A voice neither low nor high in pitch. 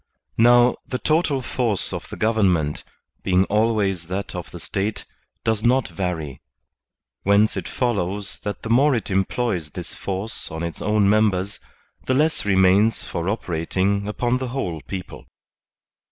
No: low, 100 Hz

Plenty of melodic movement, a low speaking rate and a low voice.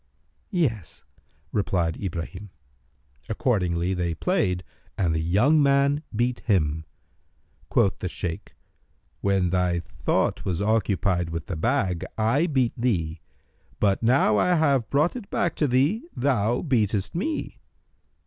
Yes: wide, 7.4 semitones; slow, 125 wpm; low, 105 Hz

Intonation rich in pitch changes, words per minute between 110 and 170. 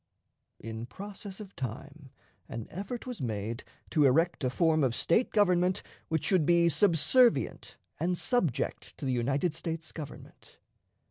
Yes: wide, 5.9 semitones; average, 140 wpm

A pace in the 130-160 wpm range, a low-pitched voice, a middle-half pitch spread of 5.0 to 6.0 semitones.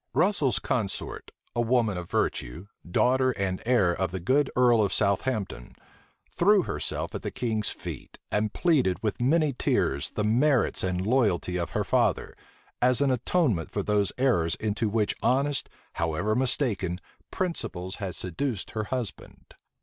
Yes: average, 150 wpm; low, 110 Hz; wide, 5.6 semitones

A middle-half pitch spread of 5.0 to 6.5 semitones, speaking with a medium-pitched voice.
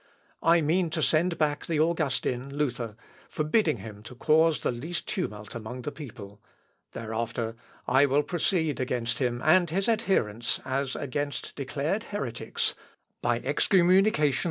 Yes: wide, 5.5 semitones; medium, 145 Hz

